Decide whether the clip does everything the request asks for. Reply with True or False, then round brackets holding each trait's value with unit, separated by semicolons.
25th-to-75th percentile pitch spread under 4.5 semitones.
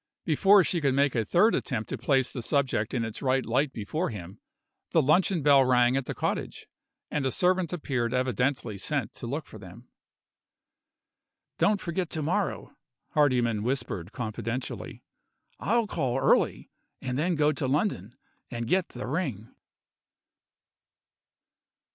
False (4.8 semitones)